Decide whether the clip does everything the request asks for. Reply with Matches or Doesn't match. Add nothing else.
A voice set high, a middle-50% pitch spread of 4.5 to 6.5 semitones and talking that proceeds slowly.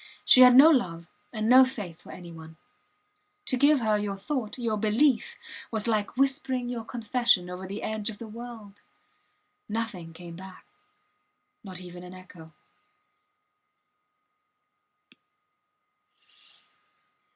Matches